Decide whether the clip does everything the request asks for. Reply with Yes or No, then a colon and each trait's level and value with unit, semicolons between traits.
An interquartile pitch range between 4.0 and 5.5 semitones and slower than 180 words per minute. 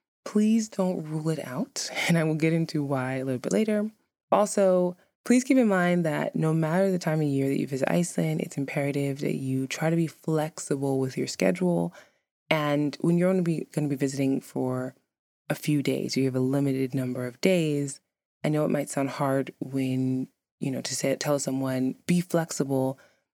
No: average, 4.5 semitones; average, 195 wpm